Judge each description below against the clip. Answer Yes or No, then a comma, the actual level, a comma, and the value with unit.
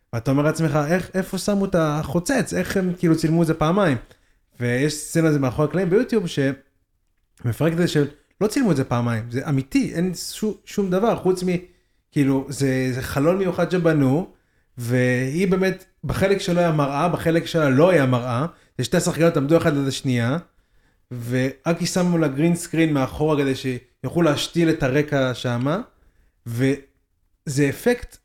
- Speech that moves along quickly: Yes, fast, 160 wpm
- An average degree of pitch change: Yes, average, 4.9 semitones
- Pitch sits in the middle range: Yes, medium, 150 Hz